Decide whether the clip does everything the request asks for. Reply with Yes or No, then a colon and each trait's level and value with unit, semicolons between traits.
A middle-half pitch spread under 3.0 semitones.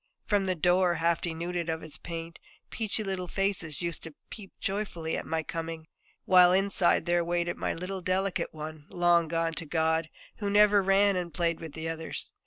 Yes: narrow, 2.6 semitones